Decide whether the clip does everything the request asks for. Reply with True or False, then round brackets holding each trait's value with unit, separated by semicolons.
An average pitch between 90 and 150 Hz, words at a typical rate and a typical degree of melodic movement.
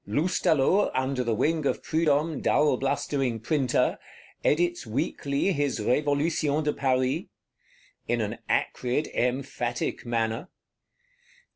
False (140 Hz; 105 wpm; 3.4 semitones)